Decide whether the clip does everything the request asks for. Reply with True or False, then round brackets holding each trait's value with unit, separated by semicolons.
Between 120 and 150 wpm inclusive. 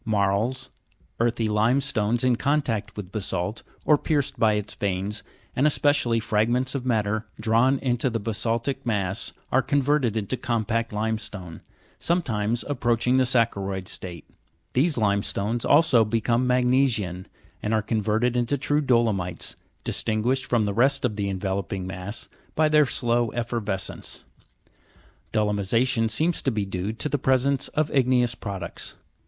True (140 wpm)